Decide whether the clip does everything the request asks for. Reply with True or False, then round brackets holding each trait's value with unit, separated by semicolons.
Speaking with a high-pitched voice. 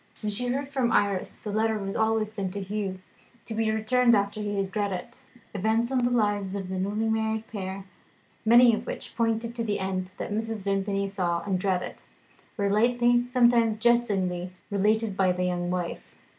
True (210 Hz)